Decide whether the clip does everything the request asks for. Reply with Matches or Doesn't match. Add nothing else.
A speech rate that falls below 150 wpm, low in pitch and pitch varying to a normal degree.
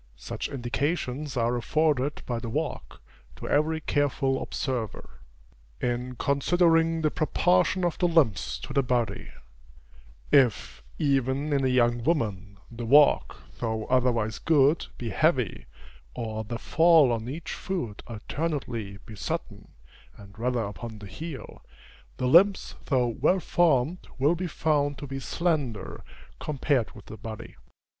Matches